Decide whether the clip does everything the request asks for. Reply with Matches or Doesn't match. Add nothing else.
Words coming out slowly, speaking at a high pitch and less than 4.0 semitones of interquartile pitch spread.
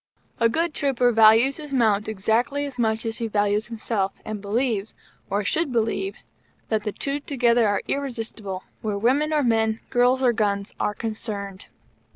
Doesn't match